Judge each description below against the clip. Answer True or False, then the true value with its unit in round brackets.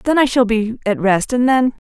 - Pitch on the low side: False (235 Hz)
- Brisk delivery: True (255 wpm)